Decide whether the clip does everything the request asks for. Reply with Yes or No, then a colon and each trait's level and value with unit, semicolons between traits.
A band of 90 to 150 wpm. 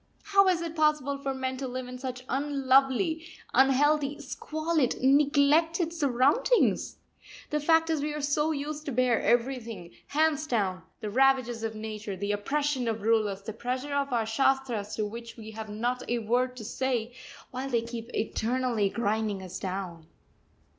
No: average, 160 wpm